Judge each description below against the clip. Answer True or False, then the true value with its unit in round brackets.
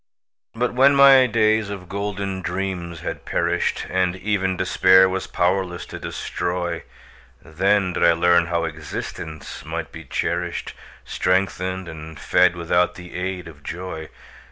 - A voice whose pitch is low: True (90 Hz)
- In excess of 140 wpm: False (135 wpm)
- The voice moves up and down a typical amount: False (2.3 semitones)